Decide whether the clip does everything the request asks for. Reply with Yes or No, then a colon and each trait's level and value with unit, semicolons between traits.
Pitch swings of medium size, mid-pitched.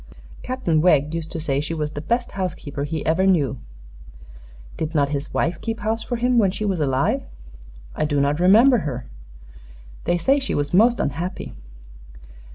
No: wide, 6.5 semitones; medium, 165 Hz